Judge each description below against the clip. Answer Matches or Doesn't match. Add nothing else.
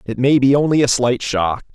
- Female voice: Doesn't match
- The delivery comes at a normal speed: Doesn't match